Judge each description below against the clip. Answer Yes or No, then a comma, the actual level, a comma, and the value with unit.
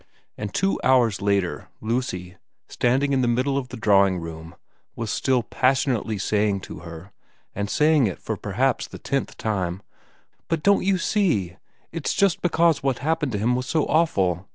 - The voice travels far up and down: Yes, wide, 6.3 semitones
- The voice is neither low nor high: No, low, 120 Hz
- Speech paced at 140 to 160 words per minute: No, average, 175 wpm